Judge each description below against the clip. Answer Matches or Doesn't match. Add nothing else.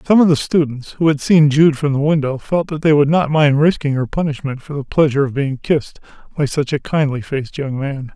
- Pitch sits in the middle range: Matches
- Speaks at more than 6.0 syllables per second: Doesn't match